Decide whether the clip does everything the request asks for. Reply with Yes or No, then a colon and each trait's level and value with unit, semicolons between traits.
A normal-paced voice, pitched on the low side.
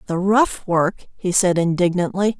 No: average, 150 wpm; medium, 185 Hz